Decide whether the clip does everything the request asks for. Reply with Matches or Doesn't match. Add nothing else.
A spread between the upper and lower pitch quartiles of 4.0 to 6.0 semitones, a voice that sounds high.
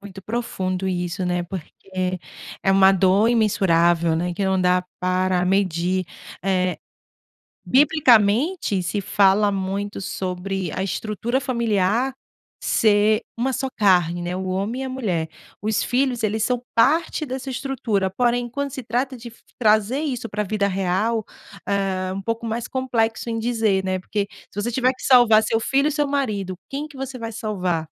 Matches